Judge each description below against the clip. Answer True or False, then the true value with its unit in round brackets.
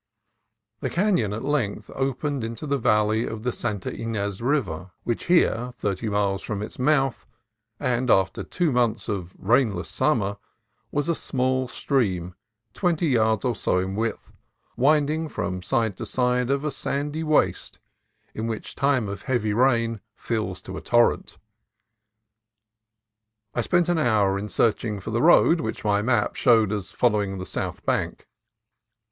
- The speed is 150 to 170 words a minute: True (155 wpm)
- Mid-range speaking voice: False (115 Hz)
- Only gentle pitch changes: False (4.9 semitones)